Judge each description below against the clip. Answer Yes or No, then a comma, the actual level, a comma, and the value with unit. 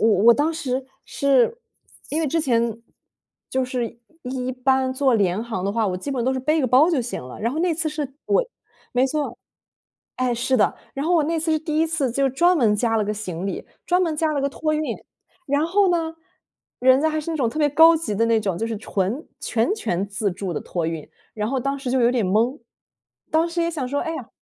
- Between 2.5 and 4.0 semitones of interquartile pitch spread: No, average, 5.3 semitones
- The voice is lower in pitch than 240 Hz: No, very high, 265 Hz